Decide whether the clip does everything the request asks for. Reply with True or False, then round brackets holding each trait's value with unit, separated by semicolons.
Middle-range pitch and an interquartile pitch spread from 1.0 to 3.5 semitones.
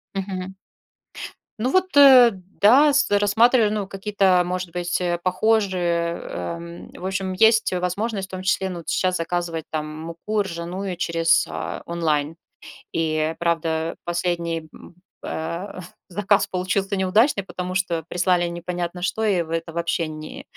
True (180 Hz; 2.8 semitones)